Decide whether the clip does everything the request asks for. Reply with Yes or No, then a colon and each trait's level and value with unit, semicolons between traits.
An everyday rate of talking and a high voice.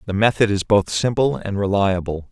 No: average, 180 wpm; low, 100 Hz